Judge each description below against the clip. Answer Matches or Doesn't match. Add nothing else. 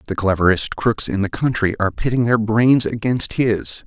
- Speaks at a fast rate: Doesn't match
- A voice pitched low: Matches